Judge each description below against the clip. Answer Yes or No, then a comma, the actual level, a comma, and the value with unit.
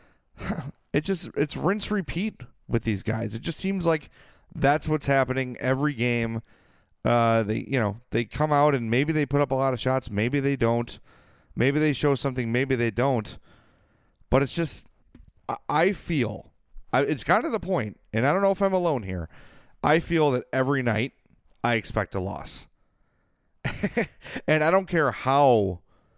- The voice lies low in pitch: Yes, low, 130 Hz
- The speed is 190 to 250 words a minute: No, average, 175 wpm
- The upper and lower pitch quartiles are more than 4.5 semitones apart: Yes, average, 4.9 semitones